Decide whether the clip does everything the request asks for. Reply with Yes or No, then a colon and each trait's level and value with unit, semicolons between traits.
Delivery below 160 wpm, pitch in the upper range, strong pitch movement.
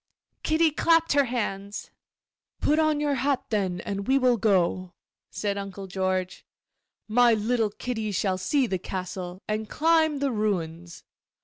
Yes: average, 140 wpm; high, 215 Hz; wide, 6.4 semitones